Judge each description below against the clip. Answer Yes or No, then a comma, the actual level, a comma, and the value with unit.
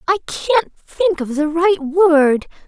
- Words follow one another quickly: No, average, 155 wpm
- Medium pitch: No, very high, 325 Hz